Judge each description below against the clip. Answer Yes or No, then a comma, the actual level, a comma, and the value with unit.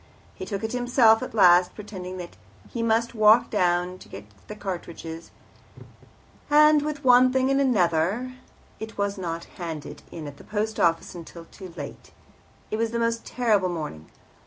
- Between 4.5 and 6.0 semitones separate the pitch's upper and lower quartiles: Yes, average, 5.2 semitones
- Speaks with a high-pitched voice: Yes, high, 205 Hz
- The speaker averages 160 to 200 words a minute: Yes, average, 170 wpm